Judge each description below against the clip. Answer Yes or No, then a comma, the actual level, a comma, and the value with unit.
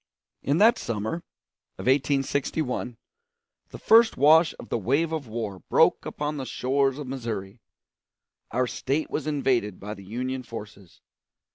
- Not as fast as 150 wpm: Yes, average, 140 wpm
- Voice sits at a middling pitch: No, low, 130 Hz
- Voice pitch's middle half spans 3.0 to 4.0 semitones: No, average, 4.5 semitones